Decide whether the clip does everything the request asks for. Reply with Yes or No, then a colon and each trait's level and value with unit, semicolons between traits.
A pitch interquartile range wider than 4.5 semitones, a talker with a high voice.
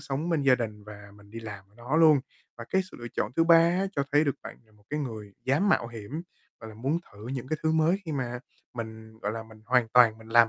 No: wide, 5.4 semitones; low, 120 Hz